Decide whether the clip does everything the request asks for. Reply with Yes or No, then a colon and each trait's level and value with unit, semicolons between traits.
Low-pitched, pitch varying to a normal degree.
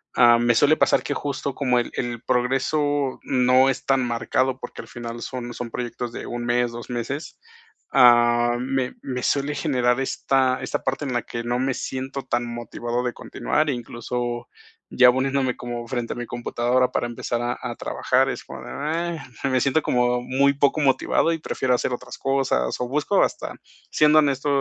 No: low, 125 Hz; narrow, 2.1 semitones